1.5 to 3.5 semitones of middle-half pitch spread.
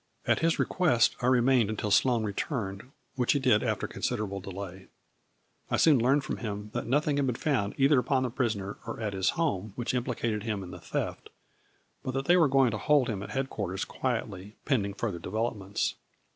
No: average, 4.7 semitones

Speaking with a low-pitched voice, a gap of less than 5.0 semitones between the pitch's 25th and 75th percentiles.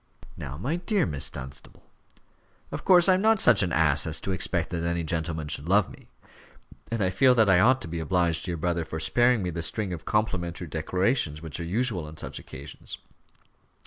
No: very low, 85 Hz; wide, 5.5 semitones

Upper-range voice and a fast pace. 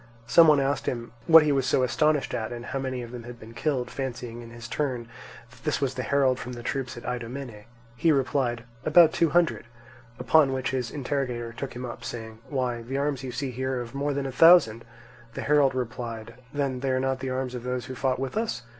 No: low, 130 Hz; fast, 230 wpm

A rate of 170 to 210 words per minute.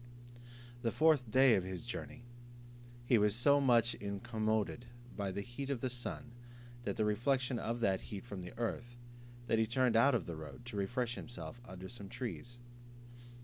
Yes: average, 175 wpm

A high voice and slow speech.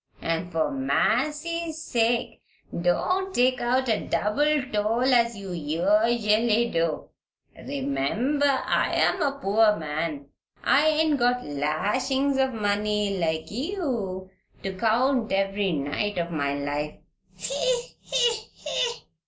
Yes: high, 215 Hz; slow, 115 wpm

